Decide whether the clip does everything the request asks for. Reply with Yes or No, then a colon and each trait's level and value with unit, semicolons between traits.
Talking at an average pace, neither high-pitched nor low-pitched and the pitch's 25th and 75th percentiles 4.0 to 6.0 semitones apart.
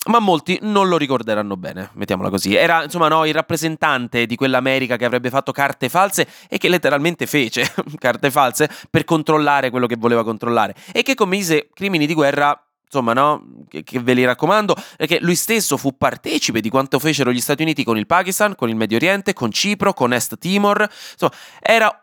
No: fast, 190 wpm; medium, 145 Hz; wide, 5.5 semitones